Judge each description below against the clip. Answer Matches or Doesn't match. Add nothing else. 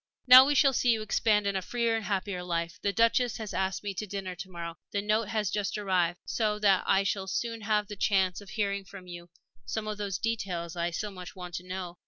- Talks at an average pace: Doesn't match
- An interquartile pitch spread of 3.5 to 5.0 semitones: Doesn't match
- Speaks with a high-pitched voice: Matches